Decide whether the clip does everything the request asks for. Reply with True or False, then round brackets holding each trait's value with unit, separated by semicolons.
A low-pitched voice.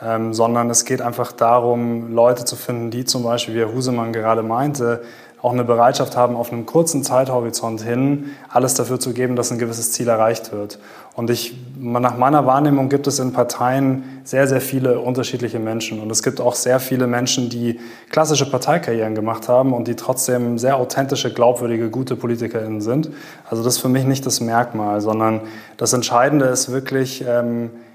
True (120 Hz)